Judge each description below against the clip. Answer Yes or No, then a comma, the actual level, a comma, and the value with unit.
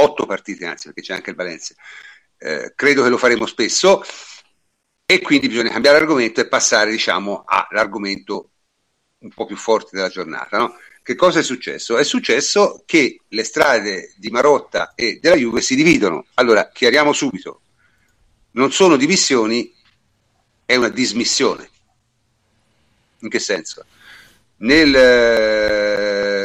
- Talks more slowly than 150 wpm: Yes, average, 135 wpm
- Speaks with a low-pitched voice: Yes, low, 125 Hz